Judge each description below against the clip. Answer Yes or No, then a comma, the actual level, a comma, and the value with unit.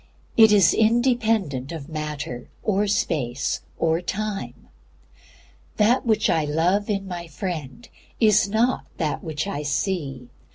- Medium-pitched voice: Yes, medium, 180 Hz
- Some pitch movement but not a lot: No, wide, 6.1 semitones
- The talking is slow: Yes, slow, 125 wpm